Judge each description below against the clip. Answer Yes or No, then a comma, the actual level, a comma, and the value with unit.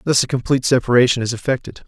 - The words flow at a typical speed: Yes, average, 190 wpm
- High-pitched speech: No, low, 125 Hz